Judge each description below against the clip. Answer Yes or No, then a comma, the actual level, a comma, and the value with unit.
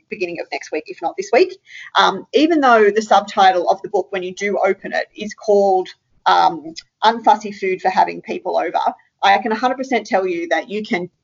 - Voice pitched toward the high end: Yes, high, 200 Hz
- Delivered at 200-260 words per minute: Yes, fast, 205 wpm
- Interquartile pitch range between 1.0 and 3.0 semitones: No, average, 3.5 semitones